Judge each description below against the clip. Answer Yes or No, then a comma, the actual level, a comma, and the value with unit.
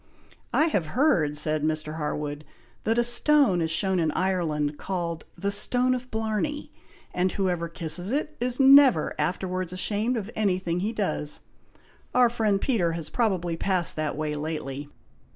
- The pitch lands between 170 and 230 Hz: Yes, medium, 185 Hz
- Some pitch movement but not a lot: No, wide, 6.3 semitones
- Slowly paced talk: No, average, 155 wpm